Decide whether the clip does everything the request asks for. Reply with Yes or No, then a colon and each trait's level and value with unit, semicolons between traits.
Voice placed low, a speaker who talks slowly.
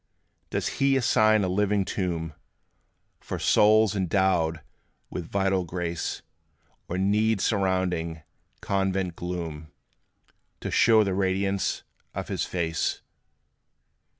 Yes: very low, 95 Hz; slow, 100 wpm